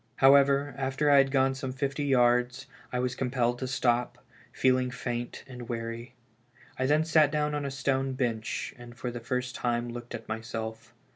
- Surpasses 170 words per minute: Yes, average, 180 wpm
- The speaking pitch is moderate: No, low, 125 Hz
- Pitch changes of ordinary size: No, narrow, 2.0 semitones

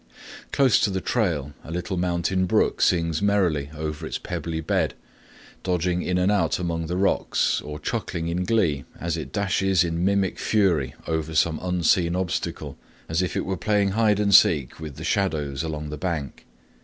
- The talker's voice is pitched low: Yes, very low, 85 Hz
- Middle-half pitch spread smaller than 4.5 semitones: Yes, average, 3.1 semitones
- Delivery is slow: No, average, 175 wpm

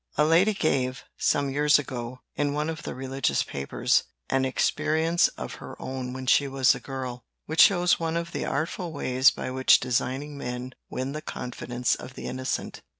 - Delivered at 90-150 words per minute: No, average, 180 wpm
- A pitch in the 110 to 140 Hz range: Yes, low, 135 Hz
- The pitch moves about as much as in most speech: Yes, average, 3.2 semitones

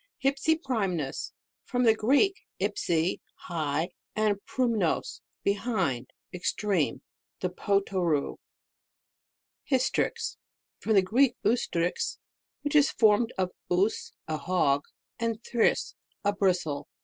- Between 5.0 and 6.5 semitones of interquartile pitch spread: Yes, average, 5.3 semitones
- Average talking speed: No, slow, 95 wpm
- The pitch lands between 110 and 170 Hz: No, high, 200 Hz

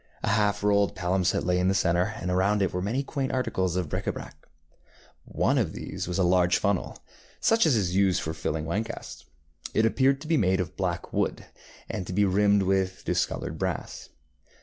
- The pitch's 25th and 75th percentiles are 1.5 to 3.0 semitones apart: Yes, narrow, 2.5 semitones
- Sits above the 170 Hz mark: No, very low, 95 Hz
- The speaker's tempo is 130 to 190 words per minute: No, average, 200 wpm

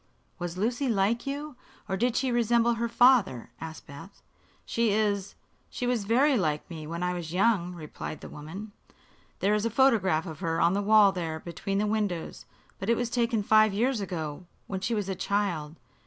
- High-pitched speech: Yes, high, 200 Hz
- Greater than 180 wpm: Yes, average, 190 wpm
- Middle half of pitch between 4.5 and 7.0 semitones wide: Yes, average, 5.1 semitones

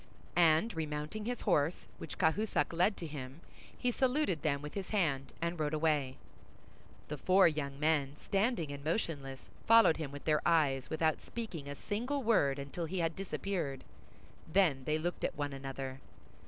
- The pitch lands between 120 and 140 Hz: No, medium, 155 Hz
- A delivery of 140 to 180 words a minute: Yes, average, 165 wpm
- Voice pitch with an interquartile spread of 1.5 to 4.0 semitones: No, average, 5.1 semitones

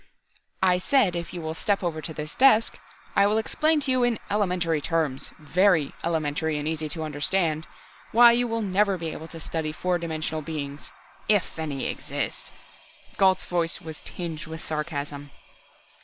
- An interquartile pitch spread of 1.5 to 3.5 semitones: No, average, 4.0 semitones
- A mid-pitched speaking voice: Yes, medium, 165 Hz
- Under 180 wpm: Yes, average, 165 wpm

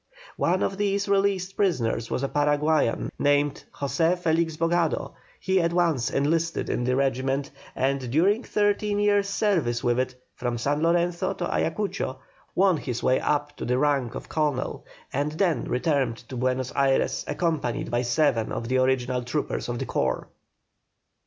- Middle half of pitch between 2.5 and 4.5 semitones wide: No, average, 5.2 semitones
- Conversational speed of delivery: Yes, average, 160 wpm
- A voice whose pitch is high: No, medium, 145 Hz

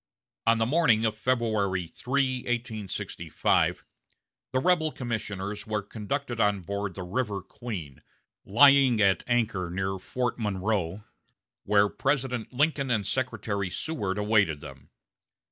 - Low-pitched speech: Yes, low, 110 Hz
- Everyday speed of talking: No, slow, 120 wpm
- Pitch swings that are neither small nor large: Yes, average, 4.0 semitones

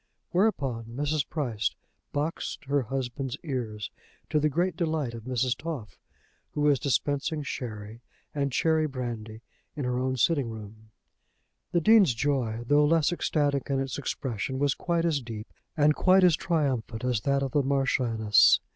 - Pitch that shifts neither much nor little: Yes, average, 4.2 semitones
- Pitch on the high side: No, low, 135 Hz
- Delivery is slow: No, average, 155 wpm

